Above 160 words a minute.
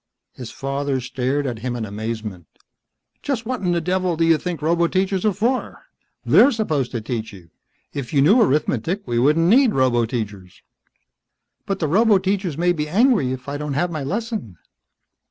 Yes: average, 170 wpm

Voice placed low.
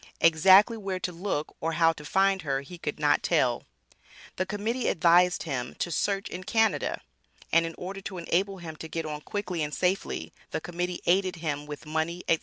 No: medium, 175 Hz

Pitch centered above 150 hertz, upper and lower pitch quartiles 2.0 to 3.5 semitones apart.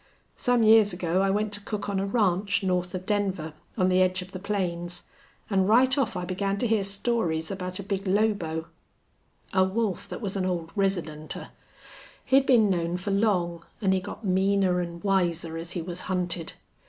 Yes: high, 190 Hz; narrow, 2.5 semitones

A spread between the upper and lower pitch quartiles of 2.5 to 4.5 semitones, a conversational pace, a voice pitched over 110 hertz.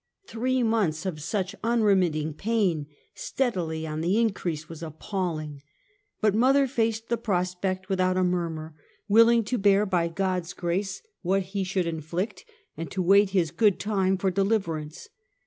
Yes: average, 4.0 semitones; average, 155 wpm; medium, 185 Hz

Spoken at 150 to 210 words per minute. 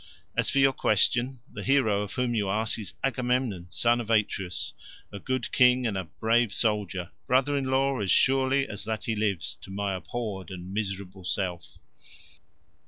Yes: average, 170 wpm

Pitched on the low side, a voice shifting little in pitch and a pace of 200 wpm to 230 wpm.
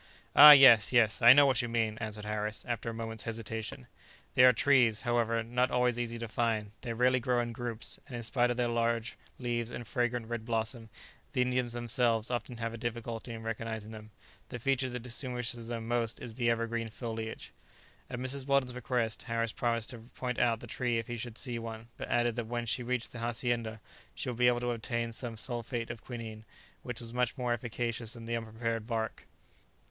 Yes: low, 120 Hz; narrow, 1.4 semitones; fast, 205 wpm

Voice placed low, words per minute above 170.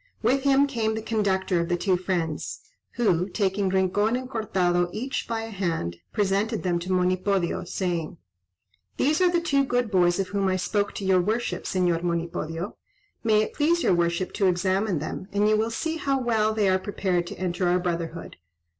No: high, 190 Hz; average, 190 wpm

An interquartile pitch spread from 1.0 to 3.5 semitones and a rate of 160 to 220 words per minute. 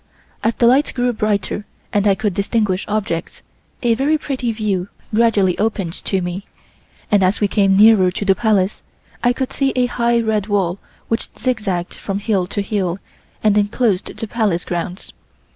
Yes: average, 3.1 semitones; average, 170 wpm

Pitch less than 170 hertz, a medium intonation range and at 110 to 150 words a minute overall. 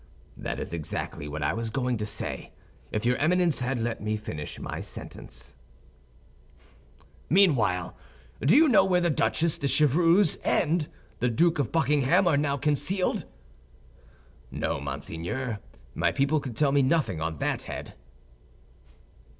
No: low, 135 Hz; wide, 7.2 semitones; average, 140 wpm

